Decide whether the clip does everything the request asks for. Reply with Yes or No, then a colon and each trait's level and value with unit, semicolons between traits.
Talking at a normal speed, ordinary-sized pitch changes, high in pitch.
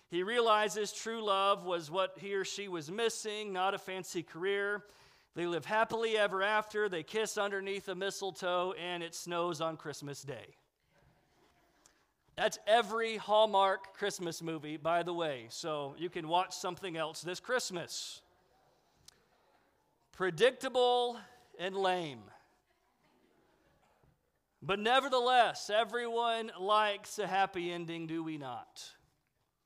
No: slow, 120 wpm; average, 3.7 semitones; high, 195 Hz